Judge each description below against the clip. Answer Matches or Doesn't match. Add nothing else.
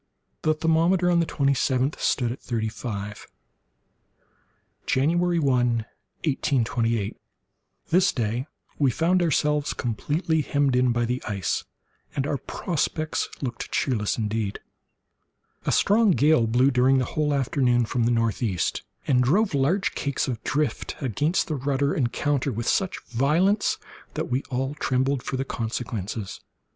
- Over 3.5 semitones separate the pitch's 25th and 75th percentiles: Matches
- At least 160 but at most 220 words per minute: Doesn't match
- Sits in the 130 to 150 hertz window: Matches